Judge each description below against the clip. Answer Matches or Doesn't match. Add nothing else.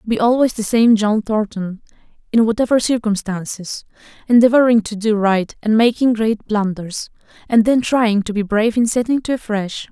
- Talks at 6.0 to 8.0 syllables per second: Doesn't match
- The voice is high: Matches